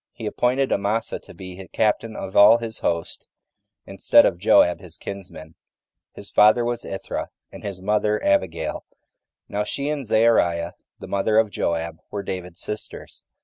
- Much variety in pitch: No, average, 3.8 semitones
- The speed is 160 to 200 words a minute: No, average, 150 wpm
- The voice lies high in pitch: No, low, 100 Hz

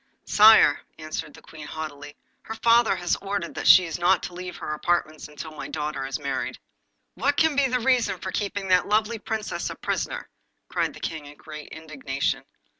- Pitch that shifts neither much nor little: No, wide, 6.2 semitones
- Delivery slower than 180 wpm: No, average, 190 wpm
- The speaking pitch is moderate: Yes, medium, 175 Hz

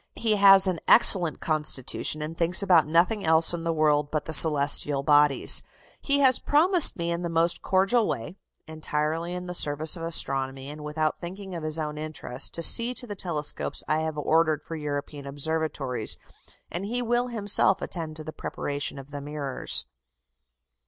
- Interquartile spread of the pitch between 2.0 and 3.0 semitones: No, average, 3.4 semitones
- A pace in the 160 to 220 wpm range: Yes, average, 175 wpm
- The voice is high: No, medium, 160 Hz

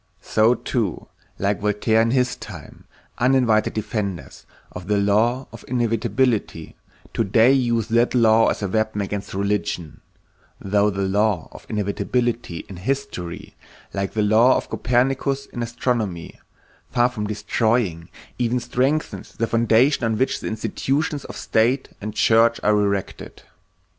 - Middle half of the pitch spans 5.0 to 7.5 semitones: No, average, 3.2 semitones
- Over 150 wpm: No, slow, 135 wpm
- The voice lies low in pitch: Yes, low, 110 Hz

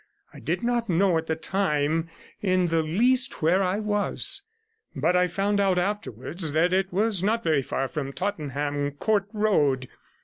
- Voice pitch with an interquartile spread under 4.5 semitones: No, average, 4.8 semitones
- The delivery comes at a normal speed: Yes, average, 165 wpm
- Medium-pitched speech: Yes, medium, 180 Hz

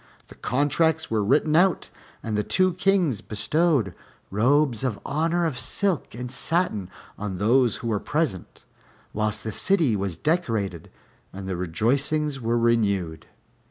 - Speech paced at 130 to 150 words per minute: Yes, average, 140 wpm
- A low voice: Yes, low, 125 Hz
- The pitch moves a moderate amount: No, wide, 7.0 semitones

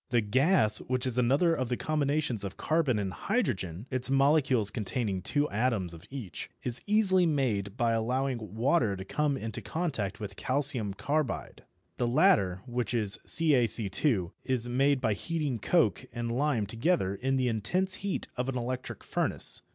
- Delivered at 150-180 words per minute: Yes, average, 160 wpm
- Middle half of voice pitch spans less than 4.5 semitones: No, average, 5.2 semitones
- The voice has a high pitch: No, low, 125 Hz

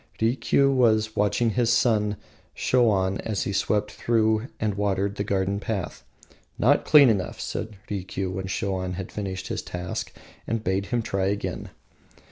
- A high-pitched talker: No, low, 100 Hz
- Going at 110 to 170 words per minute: Yes, average, 145 wpm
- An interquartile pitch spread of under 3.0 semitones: Yes, narrow, 2.6 semitones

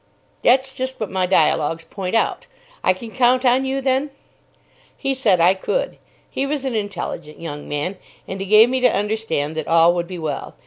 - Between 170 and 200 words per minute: Yes, average, 190 wpm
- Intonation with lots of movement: Yes, wide, 7.2 semitones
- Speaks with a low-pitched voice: No, high, 205 Hz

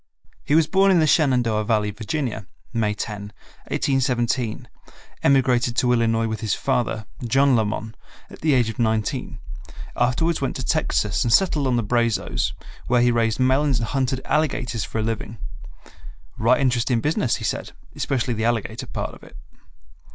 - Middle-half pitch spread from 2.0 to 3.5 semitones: Yes, average, 3.2 semitones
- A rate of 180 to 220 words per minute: No, average, 160 wpm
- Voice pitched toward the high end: No, low, 120 Hz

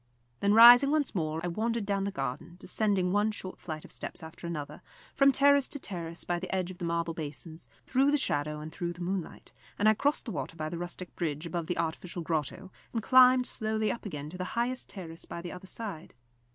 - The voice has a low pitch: No, medium, 180 Hz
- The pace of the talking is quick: Yes, fast, 220 wpm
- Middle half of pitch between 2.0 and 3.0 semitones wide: No, average, 5.0 semitones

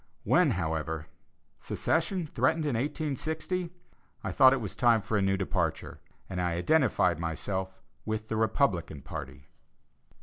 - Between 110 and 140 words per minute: Yes, slow, 135 wpm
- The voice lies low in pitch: Yes, low, 110 Hz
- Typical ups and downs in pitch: No, wide, 8.4 semitones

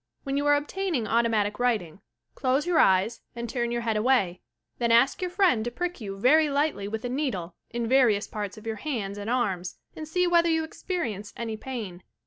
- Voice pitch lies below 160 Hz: No, high, 235 Hz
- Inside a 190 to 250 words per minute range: Yes, average, 200 wpm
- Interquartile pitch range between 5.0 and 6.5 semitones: Yes, wide, 5.6 semitones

